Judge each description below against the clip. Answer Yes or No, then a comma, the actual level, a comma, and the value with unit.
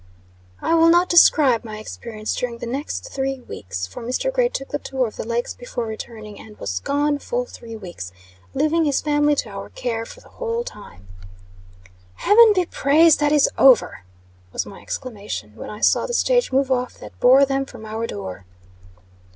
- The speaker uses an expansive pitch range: Yes, wide, 5.7 semitones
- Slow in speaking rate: No, average, 185 wpm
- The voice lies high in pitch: Yes, very high, 255 Hz